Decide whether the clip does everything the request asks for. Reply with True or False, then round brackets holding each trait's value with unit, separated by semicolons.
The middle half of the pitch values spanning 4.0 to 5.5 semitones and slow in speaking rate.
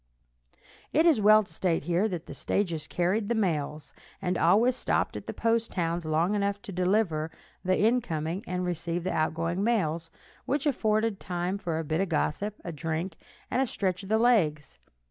False (4.5 semitones; 185 wpm)